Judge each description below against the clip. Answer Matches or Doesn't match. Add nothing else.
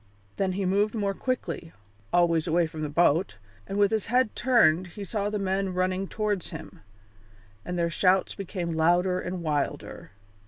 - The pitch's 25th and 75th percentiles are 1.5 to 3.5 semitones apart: Matches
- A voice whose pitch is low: Doesn't match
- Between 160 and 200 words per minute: Matches